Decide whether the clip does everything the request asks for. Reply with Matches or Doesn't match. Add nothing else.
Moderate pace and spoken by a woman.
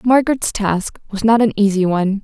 Matches